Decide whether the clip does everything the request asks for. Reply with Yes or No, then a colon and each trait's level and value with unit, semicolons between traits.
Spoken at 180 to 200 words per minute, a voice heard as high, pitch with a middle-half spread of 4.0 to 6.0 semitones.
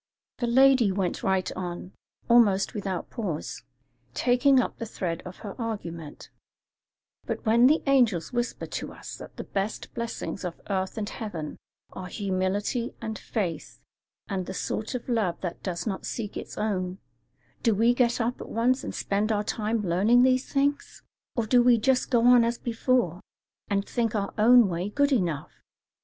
No: average, 170 wpm; high, 215 Hz; average, 4.4 semitones